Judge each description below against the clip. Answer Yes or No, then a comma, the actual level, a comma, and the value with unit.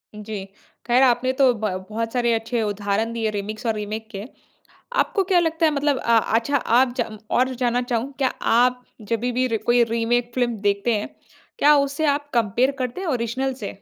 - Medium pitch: No, high, 240 Hz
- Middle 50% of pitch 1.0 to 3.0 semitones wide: Yes, average, 2.7 semitones